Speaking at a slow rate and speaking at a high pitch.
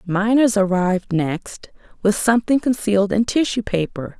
Yes: slow, 130 wpm; high, 205 Hz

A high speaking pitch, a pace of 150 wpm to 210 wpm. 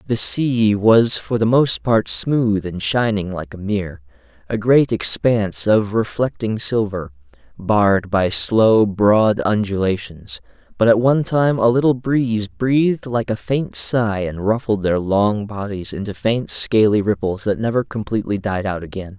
No: low, 105 Hz; average, 160 wpm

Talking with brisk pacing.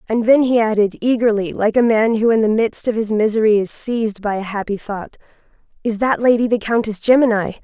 Yes: fast, 210 wpm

